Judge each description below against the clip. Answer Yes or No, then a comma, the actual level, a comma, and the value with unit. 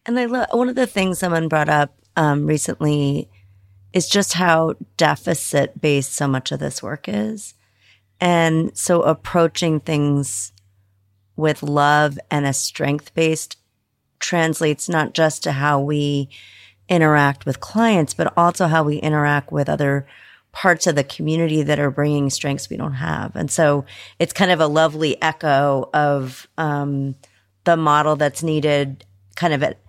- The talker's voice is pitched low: No, medium, 150 Hz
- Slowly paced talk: No, average, 155 wpm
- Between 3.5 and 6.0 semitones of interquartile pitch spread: No, average, 2.9 semitones